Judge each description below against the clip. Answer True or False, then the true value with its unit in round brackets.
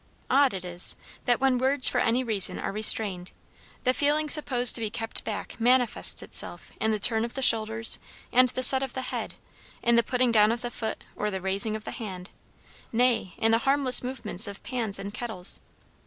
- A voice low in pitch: False (230 Hz)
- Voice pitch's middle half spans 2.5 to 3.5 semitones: True (3.2 semitones)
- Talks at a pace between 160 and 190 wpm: False (200 wpm)